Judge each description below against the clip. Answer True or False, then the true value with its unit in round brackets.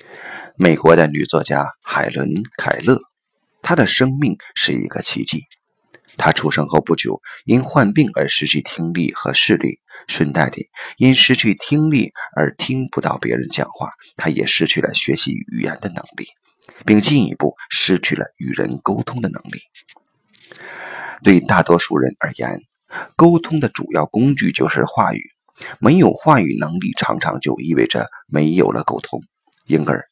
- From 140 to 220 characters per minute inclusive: False (230 characters per minute)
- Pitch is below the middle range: True (105 Hz)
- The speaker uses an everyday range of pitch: False (8.0 semitones)